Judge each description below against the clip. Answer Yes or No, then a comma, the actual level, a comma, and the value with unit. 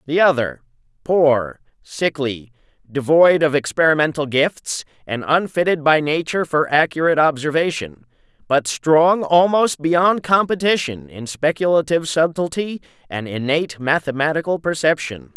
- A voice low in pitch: No, medium, 155 Hz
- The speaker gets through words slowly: Yes, slow, 105 wpm